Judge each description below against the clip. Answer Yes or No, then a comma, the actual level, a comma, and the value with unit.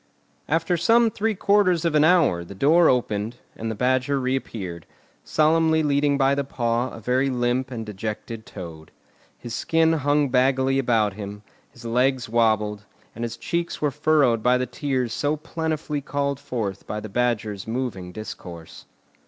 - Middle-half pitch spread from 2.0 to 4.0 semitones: No, average, 4.9 semitones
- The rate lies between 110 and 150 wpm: No, average, 160 wpm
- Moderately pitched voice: No, low, 125 Hz